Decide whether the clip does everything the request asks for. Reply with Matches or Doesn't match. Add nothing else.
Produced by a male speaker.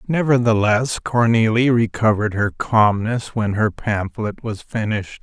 Matches